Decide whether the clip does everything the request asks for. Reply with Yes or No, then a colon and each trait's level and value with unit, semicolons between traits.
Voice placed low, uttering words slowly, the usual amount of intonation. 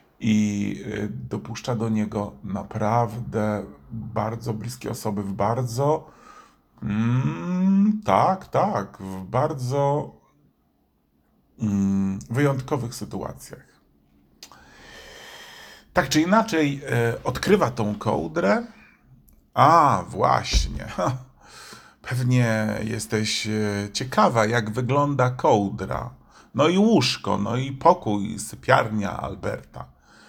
Yes: low, 110 Hz; slow, 80 wpm; average, 3.8 semitones